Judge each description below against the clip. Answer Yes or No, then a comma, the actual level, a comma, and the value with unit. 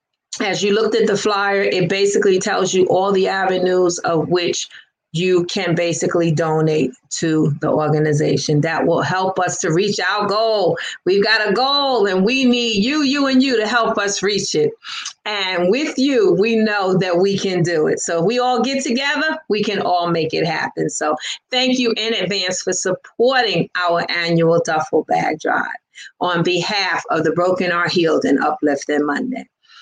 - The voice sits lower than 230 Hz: Yes, high, 190 Hz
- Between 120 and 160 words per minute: No, average, 180 wpm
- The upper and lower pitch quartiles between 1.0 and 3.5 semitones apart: No, average, 5.3 semitones